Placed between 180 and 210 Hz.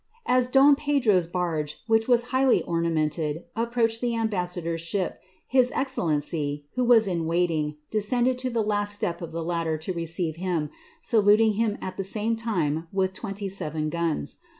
Yes: high, 190 Hz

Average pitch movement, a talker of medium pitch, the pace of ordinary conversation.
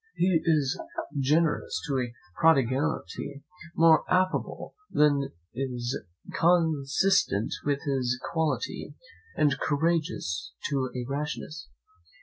No: average, 3.5 semitones; medium, 145 Hz; slow, 95 wpm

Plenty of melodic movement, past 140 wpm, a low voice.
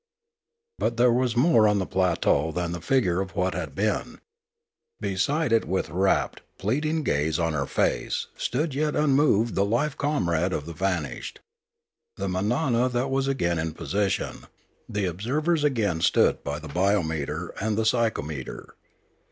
Yes: wide, 6.9 semitones; average, 150 wpm; low, 100 Hz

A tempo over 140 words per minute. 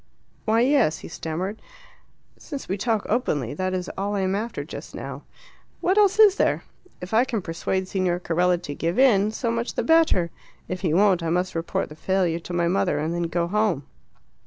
Yes: average, 200 wpm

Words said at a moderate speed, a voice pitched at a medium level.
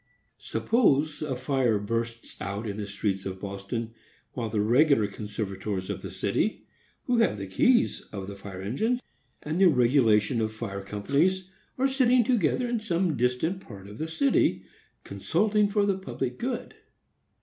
No: average, 160 wpm; low, 125 Hz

